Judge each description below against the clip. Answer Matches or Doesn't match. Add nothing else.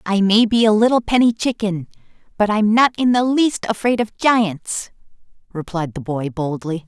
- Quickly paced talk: Doesn't match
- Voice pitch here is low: Doesn't match